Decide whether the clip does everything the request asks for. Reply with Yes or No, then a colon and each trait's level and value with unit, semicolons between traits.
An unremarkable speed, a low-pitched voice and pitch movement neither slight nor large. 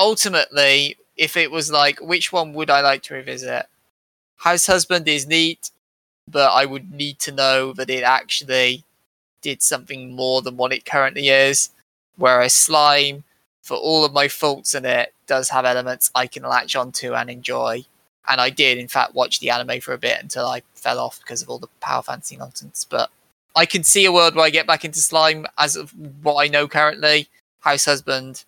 No: average, 195 wpm; medium, 145 Hz; average, 3.4 semitones